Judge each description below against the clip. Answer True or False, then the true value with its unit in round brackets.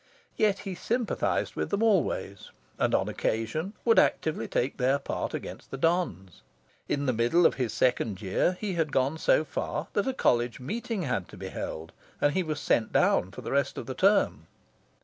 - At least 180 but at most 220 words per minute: True (190 wpm)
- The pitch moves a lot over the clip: True (7.7 semitones)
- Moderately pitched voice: True (145 Hz)